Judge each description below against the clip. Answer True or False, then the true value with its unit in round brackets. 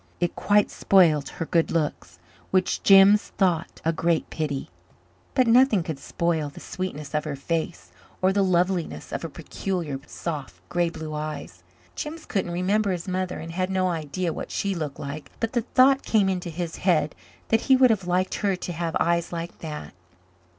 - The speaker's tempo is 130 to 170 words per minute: False (180 wpm)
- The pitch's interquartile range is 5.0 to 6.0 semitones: False (3.3 semitones)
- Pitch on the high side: False (175 Hz)